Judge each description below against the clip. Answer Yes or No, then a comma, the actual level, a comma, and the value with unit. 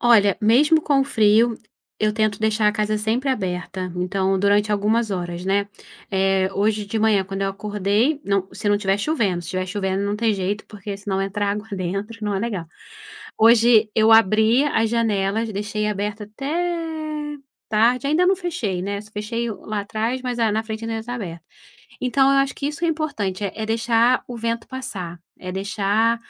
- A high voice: Yes, high, 215 Hz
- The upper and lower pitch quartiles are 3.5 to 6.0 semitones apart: No, average, 2.9 semitones